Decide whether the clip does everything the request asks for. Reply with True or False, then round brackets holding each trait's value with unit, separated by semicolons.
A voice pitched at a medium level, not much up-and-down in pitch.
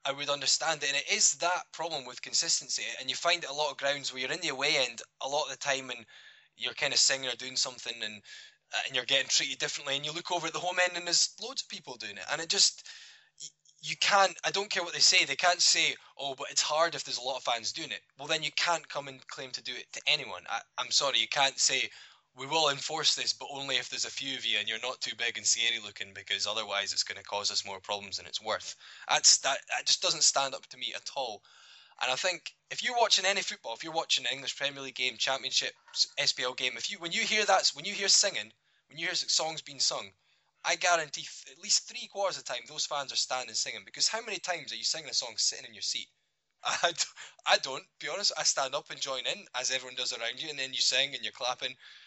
False (145 Hz; 5.1 semitones)